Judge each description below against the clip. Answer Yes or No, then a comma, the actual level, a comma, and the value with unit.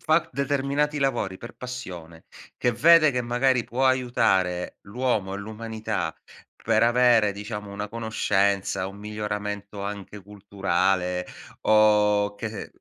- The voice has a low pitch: Yes, low, 105 Hz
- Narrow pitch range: No, average, 3.6 semitones